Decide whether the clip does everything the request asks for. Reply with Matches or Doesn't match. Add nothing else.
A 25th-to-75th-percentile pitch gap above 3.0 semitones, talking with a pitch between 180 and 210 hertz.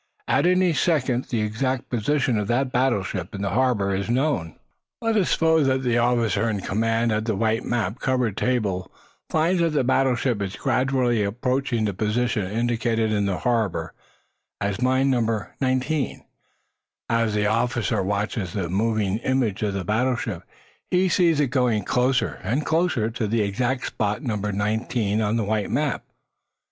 Doesn't match